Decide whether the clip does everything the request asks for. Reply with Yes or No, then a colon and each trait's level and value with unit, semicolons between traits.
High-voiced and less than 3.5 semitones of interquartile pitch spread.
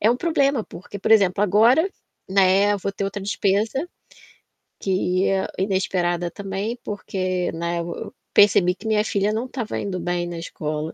Yes: high, 195 Hz; average, 2.8 semitones